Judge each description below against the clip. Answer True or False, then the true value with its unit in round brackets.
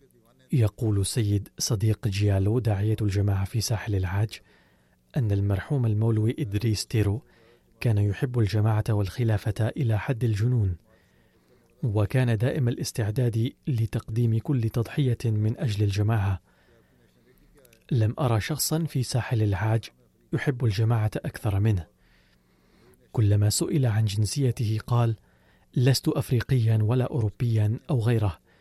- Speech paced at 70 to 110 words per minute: True (105 wpm)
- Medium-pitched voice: False (110 Hz)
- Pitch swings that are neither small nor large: True (3.0 semitones)